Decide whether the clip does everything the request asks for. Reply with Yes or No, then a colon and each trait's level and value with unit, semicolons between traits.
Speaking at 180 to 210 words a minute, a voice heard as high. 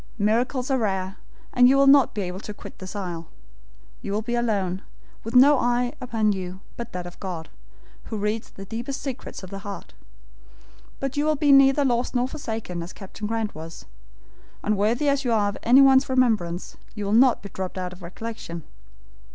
Yes: average, 190 wpm; high, 220 Hz